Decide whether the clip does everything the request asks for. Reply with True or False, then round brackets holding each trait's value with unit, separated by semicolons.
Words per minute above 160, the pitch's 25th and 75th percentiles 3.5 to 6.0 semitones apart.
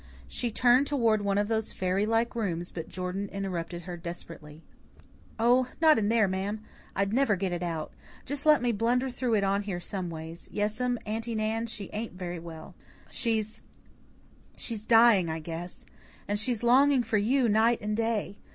True (170 wpm; 4.3 semitones)